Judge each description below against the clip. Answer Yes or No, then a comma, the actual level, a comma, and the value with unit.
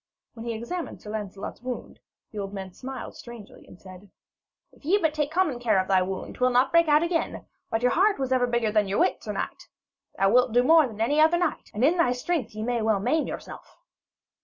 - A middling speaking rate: No, fast, 235 wpm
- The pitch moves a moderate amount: No, wide, 6.4 semitones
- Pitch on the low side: No, high, 245 Hz